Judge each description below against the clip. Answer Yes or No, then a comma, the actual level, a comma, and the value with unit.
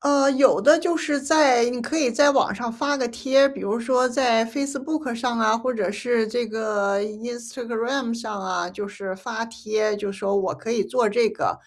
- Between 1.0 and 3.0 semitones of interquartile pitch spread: No, average, 3.7 semitones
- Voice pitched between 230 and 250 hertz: Yes, high, 235 Hz